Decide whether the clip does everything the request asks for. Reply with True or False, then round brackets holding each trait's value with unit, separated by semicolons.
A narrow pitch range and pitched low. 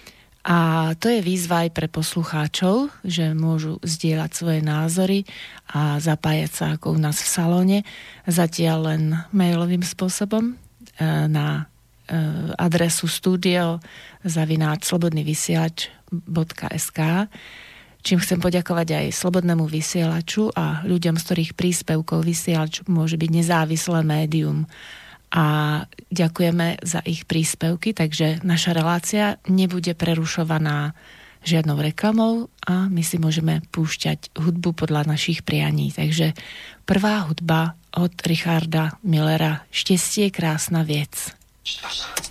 False (2.0 semitones; 165 Hz)